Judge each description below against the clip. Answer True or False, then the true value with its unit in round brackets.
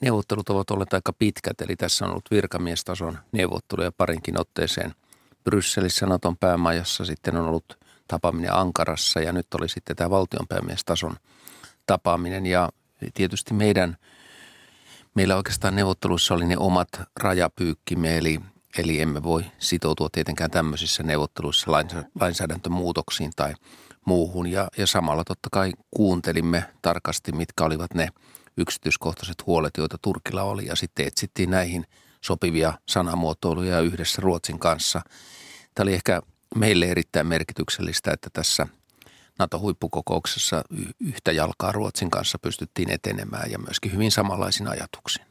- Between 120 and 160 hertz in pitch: False (90 Hz)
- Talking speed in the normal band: True (125 wpm)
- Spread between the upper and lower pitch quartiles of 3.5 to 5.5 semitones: False (2.7 semitones)